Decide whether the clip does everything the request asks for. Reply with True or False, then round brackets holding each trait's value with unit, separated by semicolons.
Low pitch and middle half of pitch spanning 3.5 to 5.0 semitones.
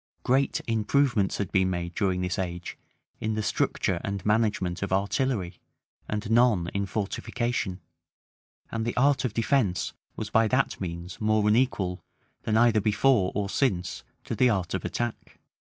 True (105 Hz; 4.0 semitones)